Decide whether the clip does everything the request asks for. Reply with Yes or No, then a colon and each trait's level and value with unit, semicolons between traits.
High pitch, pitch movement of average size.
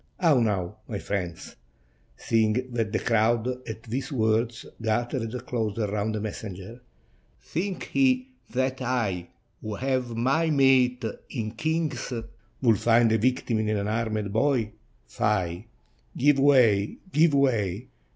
No: low, 115 Hz; average, 3.4 semitones